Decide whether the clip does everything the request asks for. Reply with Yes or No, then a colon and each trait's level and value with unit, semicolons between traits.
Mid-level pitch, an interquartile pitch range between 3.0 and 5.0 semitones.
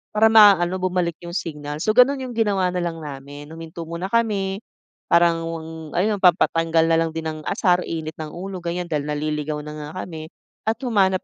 Yes: medium, 170 Hz; average, 3.3 semitones